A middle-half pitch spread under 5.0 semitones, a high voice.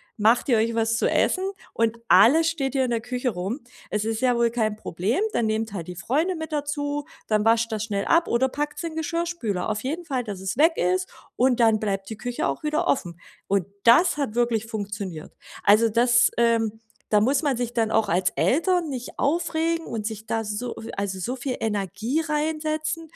No: wide, 5.4 semitones; high, 235 Hz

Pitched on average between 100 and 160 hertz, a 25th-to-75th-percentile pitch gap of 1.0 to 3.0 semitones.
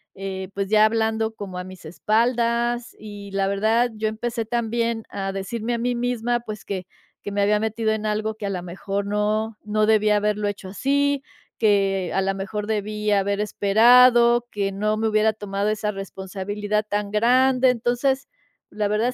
No: high, 215 Hz; narrow, 2.5 semitones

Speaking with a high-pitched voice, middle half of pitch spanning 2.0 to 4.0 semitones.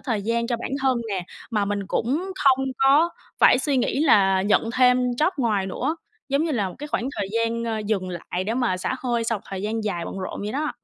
No: high, 230 Hz; average, 4.9 semitones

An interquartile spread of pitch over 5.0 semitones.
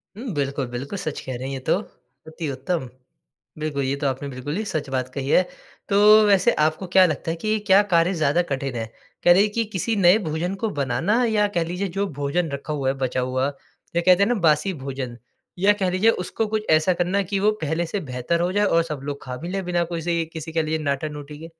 Yes: wide, 5.4 semitones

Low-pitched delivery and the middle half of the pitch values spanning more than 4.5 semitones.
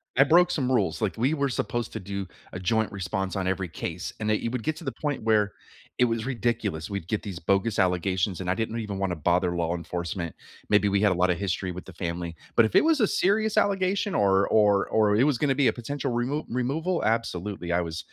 Yes: low, 105 Hz; average, 5.3 semitones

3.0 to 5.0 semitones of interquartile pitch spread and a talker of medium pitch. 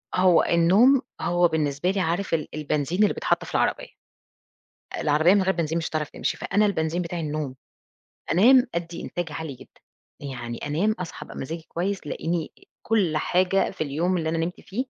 Yes: average, 3.3 semitones; medium, 170 Hz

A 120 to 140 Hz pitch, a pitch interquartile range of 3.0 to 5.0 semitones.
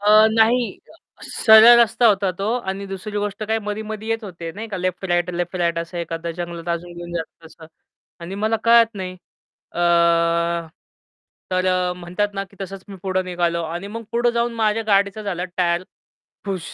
No: high, 190 Hz; average, 3.7 semitones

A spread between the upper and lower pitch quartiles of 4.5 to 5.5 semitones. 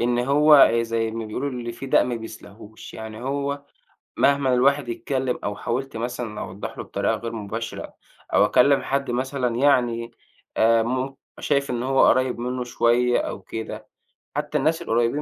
No: average, 2.9 semitones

